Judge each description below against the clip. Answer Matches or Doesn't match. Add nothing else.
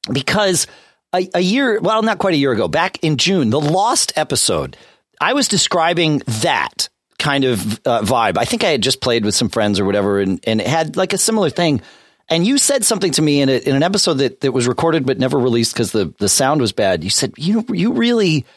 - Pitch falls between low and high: Matches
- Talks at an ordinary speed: Doesn't match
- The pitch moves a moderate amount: Doesn't match